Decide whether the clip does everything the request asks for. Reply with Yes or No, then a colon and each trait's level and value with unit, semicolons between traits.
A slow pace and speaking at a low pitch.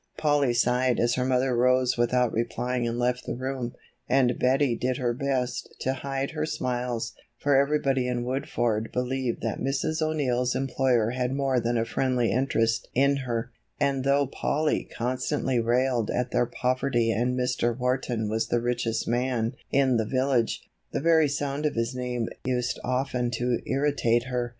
No: average, 165 wpm; low, 125 Hz